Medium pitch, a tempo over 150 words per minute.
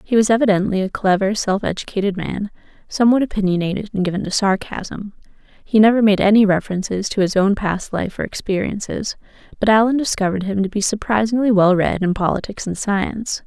No: high, 205 Hz; average, 175 wpm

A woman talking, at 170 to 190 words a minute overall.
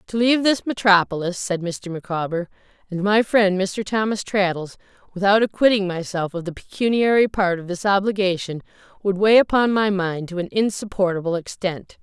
No: female; average, 160 wpm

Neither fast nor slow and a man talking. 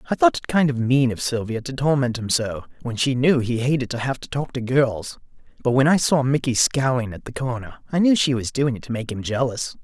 No: fast, 255 wpm; male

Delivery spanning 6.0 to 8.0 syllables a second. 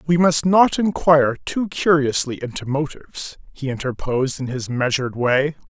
No: 5.0 syllables/s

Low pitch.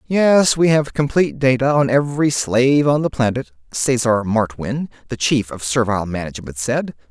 Yes: low, 125 Hz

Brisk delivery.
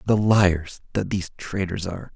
No: average, 165 wpm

